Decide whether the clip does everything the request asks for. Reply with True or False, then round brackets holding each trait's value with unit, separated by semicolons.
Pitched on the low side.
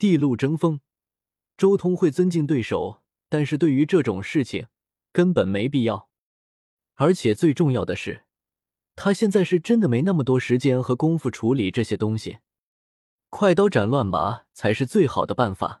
False (145 Hz)